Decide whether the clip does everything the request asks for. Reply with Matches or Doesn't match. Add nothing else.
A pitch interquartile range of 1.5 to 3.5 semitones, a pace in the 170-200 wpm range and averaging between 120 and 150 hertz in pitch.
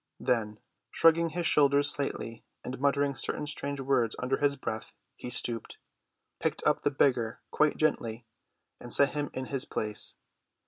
Doesn't match